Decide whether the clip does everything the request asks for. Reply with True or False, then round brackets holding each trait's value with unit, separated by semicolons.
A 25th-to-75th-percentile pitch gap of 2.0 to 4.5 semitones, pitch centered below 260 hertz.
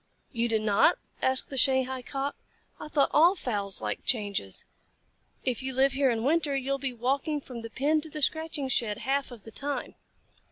False (3.2 semitones; 265 Hz)